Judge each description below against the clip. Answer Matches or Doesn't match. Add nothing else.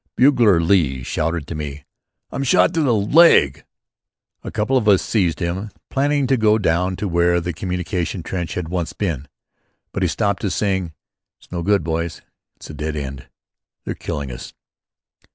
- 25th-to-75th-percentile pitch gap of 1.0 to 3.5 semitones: Doesn't match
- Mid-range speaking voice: Doesn't match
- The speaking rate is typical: Matches